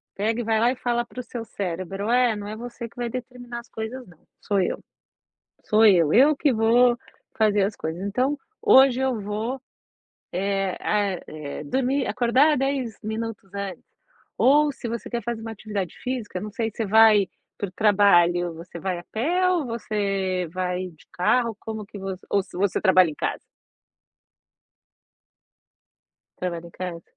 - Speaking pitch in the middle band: No, high, 215 Hz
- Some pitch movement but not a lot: Yes, average, 4.2 semitones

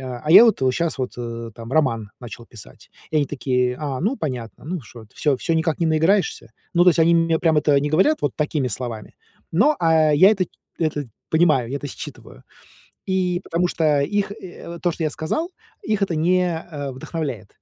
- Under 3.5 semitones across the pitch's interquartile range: No, average, 5.1 semitones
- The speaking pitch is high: No, medium, 155 Hz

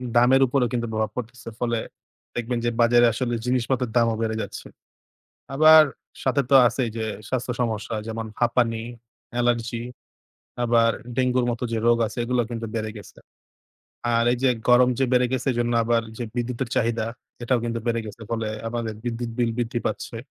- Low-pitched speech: Yes, low, 120 Hz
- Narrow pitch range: Yes, narrow, 1.3 semitones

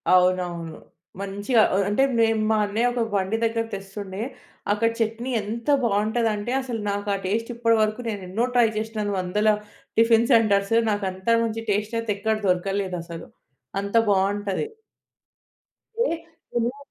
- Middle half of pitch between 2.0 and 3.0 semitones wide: Yes, narrow, 2.5 semitones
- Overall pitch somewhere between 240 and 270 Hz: No, high, 210 Hz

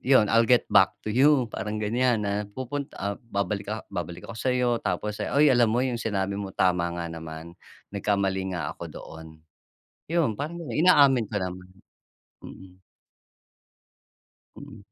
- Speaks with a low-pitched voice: Yes, low, 105 Hz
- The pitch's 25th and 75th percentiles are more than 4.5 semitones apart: Yes, average, 4.9 semitones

